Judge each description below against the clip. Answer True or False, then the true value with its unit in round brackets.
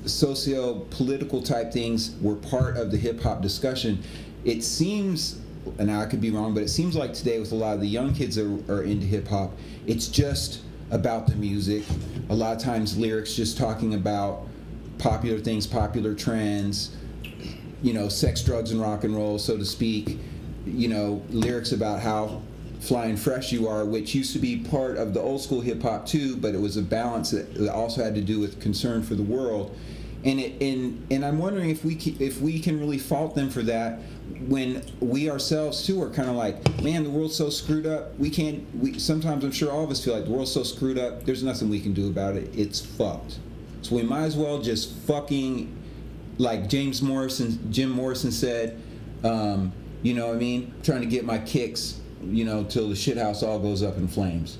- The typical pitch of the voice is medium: False (115 Hz)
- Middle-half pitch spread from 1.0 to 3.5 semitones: False (4.3 semitones)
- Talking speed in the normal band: False (210 wpm)